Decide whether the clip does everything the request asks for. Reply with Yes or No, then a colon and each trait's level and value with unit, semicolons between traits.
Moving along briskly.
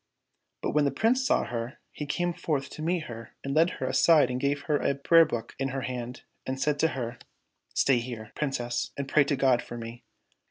Yes: fast, 225 wpm